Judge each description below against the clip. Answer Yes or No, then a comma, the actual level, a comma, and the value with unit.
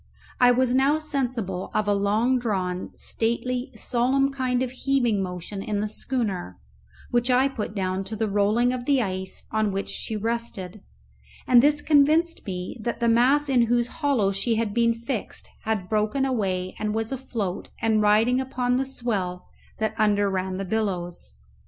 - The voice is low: No, high, 225 Hz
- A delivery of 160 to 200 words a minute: Yes, average, 170 wpm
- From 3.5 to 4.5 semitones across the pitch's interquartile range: Yes, average, 4.0 semitones